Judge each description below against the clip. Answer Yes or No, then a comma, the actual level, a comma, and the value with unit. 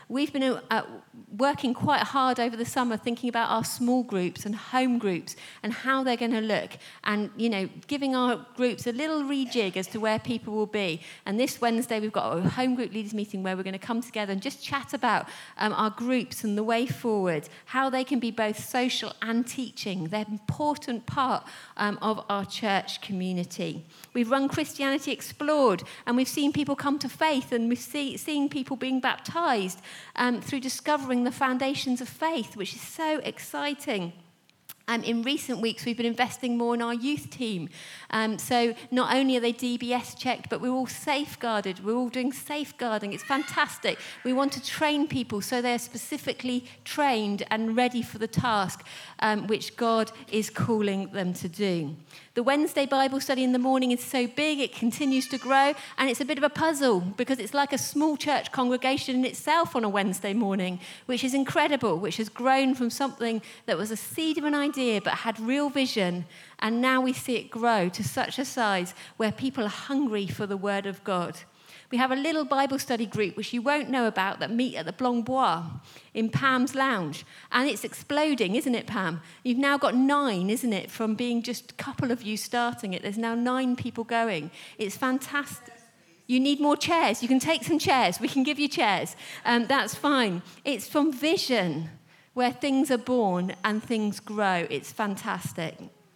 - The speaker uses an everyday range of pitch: Yes, average, 4.1 semitones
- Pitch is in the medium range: No, high, 240 Hz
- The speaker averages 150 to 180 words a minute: No, average, 195 wpm